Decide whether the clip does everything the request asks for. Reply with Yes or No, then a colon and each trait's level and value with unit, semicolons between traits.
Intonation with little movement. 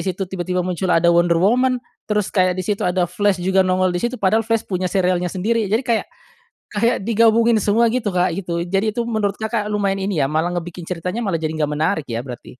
No: average, 3.5 semitones